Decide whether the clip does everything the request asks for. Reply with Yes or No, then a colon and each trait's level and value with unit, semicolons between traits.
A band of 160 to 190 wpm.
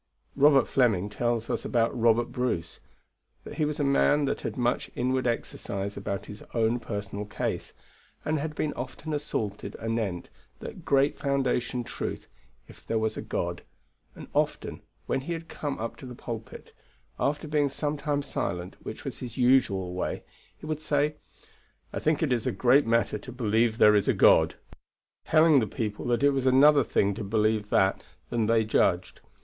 Yes: average, 175 wpm